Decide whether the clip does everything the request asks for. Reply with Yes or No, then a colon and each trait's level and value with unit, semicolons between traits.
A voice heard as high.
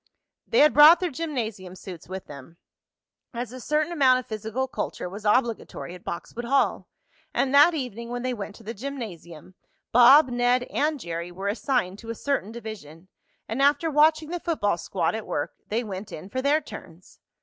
Yes: high, 235 Hz